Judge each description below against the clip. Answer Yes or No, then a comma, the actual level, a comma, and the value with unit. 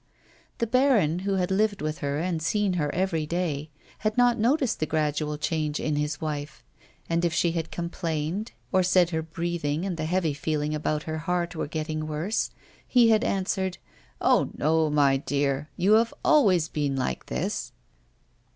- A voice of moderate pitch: Yes, medium, 165 Hz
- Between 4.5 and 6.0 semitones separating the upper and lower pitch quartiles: No, average, 3.8 semitones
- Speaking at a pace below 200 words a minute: Yes, average, 170 wpm